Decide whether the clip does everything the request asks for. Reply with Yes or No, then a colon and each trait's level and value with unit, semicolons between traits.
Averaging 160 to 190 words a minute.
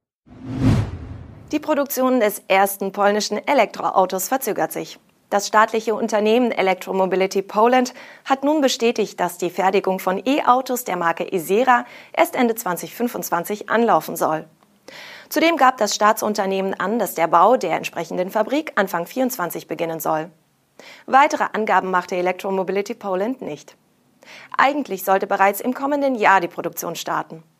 No: average, 130 wpm